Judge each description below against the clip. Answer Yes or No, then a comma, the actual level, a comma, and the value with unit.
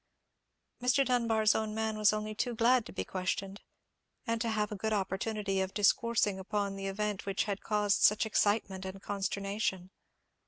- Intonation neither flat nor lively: No, narrow, 2.0 semitones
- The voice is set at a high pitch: Yes, high, 210 Hz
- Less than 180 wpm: Yes, average, 165 wpm